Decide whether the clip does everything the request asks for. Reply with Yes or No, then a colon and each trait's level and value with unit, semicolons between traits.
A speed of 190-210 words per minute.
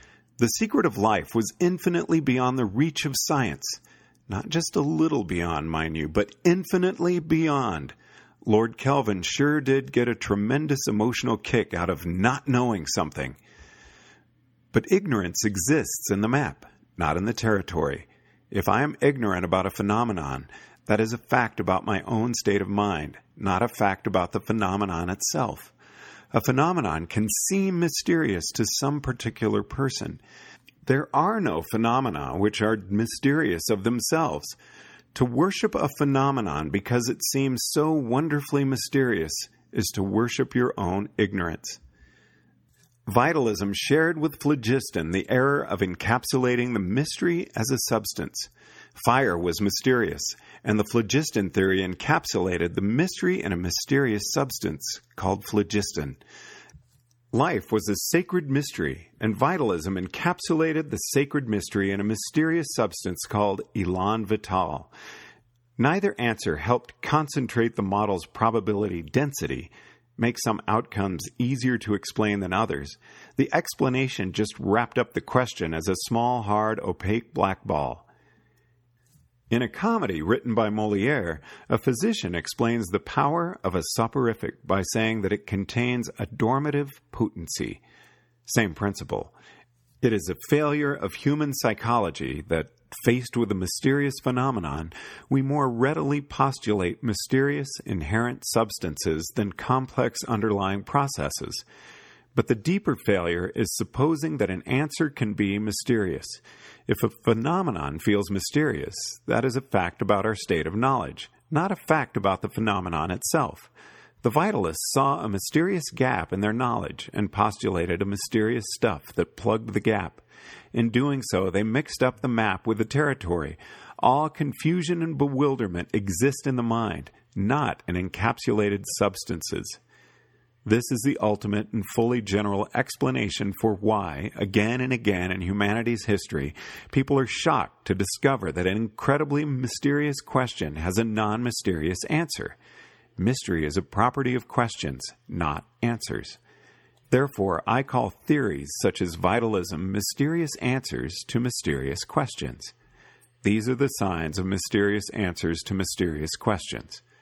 No: average, 140 wpm